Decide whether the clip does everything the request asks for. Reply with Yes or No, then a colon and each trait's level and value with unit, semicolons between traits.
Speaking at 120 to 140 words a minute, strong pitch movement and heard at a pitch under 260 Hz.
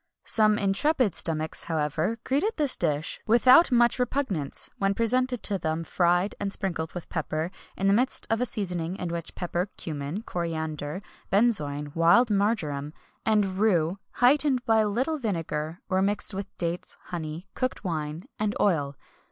No: average, 160 wpm; wide, 5.7 semitones; high, 190 Hz